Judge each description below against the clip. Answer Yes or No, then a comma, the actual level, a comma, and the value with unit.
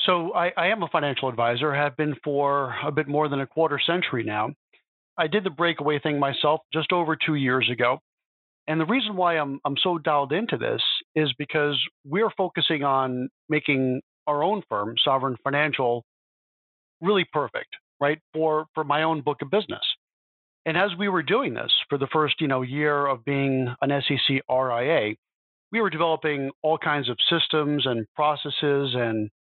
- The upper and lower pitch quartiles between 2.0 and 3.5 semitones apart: Yes, average, 3.1 semitones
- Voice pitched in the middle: Yes, medium, 150 Hz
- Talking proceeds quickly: No, average, 175 wpm